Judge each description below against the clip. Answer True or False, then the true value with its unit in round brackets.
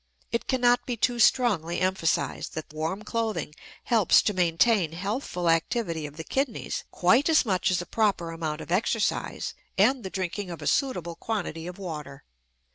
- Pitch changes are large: True (5.7 semitones)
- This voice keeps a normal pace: True (165 wpm)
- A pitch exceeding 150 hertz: True (185 Hz)